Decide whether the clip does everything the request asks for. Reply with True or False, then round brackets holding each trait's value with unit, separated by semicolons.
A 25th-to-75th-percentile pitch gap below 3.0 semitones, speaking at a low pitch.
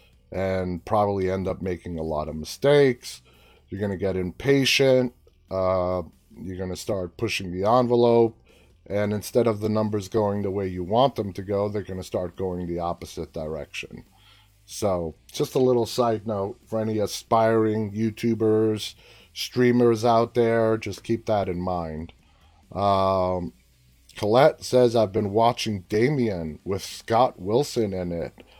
False (4.0 semitones; 100 Hz)